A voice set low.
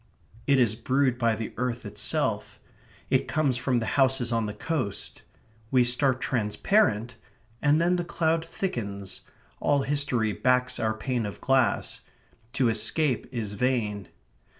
Yes: low, 125 Hz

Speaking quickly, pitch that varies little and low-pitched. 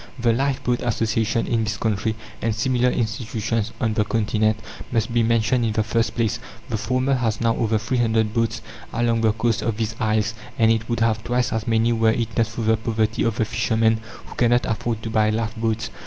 Yes: fast, 210 wpm; narrow, 1.0 semitones; low, 115 Hz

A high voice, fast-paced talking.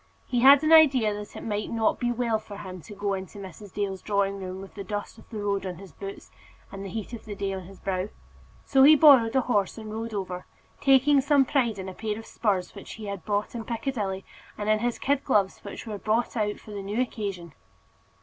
Yes: high, 210 Hz; fast, 235 wpm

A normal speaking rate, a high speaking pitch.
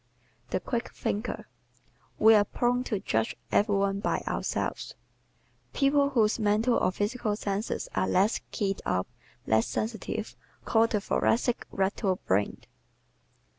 No: slow, 130 wpm; high, 210 Hz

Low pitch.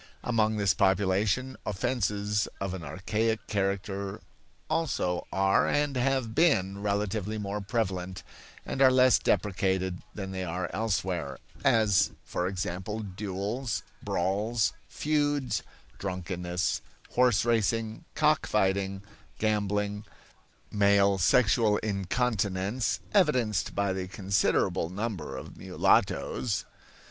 Yes: low, 100 Hz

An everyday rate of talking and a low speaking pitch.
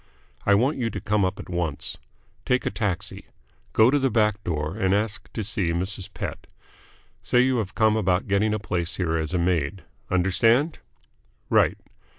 Yes: average, 175 wpm; low, 100 Hz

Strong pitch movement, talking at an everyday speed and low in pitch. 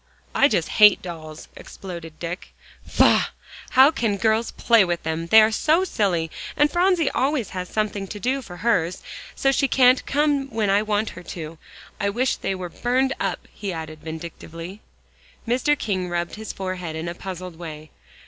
No: wide, 6.2 semitones; average, 170 wpm; high, 195 Hz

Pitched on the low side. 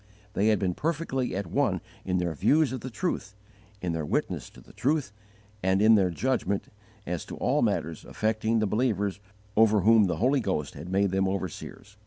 Yes: low, 100 Hz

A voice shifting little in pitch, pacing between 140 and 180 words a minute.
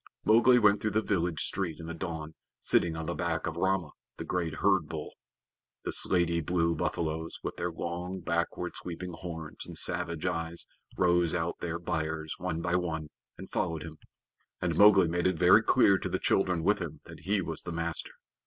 No: narrow, 1.8 semitones; average, 190 wpm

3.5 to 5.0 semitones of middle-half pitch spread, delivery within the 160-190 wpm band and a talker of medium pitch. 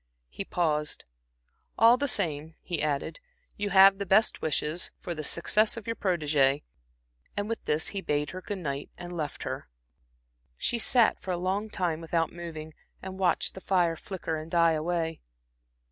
Yes: average, 3.9 semitones; average, 170 wpm; medium, 175 Hz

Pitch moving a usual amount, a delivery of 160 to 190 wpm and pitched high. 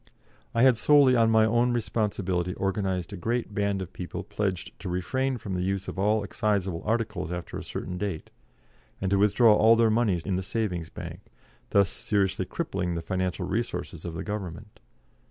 No: average, 3.4 semitones; average, 180 wpm; low, 100 Hz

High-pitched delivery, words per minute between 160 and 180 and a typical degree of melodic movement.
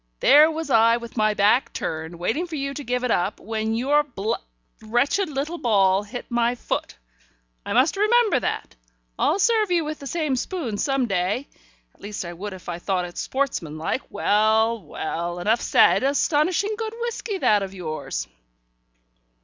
No: high, 240 Hz; average, 170 wpm; wide, 6.8 semitones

